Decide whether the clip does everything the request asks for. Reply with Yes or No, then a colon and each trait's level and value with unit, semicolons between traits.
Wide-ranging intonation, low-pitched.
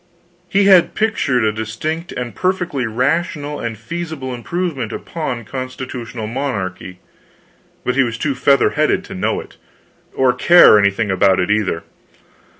Yes: wide, 6.2 semitones; low, 125 Hz